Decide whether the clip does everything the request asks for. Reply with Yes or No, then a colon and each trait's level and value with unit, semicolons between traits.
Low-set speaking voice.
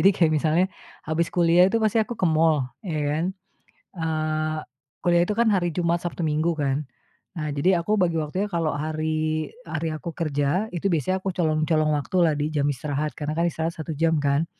No: medium, 160 Hz